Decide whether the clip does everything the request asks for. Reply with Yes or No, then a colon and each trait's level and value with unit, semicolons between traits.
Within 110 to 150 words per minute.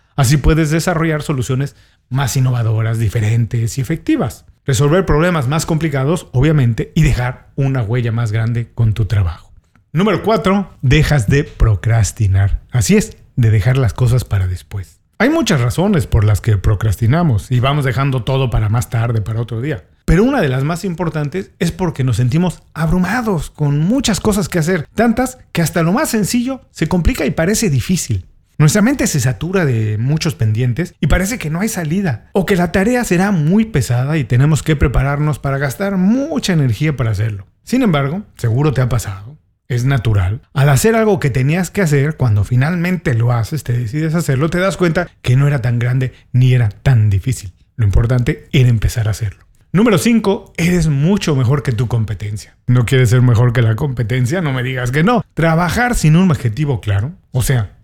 No: average, 185 wpm